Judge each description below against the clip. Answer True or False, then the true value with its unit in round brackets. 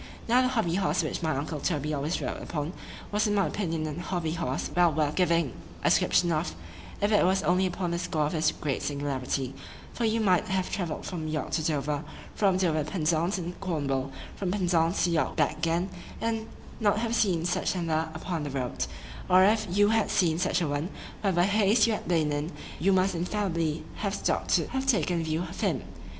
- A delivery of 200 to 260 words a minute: True (205 wpm)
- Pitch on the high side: False (170 Hz)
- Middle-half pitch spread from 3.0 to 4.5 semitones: True (3.8 semitones)